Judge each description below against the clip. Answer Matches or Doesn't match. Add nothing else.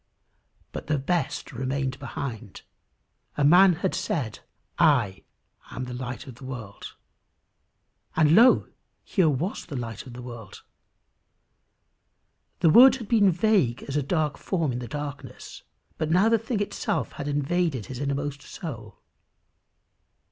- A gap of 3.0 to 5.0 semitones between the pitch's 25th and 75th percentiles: Doesn't match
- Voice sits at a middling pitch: Matches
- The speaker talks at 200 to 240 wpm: Doesn't match